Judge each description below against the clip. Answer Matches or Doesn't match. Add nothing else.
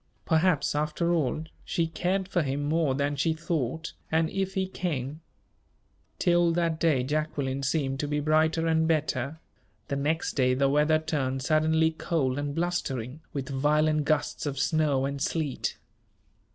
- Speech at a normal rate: Matches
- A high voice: Doesn't match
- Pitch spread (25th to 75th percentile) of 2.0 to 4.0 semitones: Matches